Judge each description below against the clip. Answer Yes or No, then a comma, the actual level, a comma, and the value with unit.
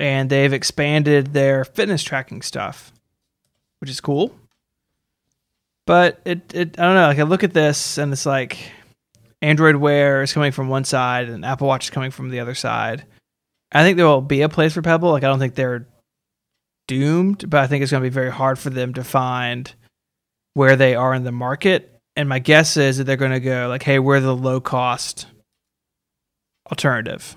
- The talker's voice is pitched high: No, low, 135 Hz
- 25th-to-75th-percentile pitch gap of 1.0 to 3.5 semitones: Yes, narrow, 2.4 semitones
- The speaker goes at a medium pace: Yes, average, 195 wpm